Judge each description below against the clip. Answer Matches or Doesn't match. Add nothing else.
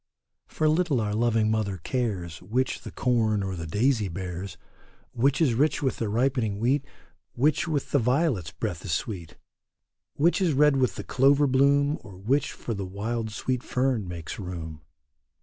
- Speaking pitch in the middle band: Doesn't match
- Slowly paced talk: Doesn't match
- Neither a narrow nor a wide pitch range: Doesn't match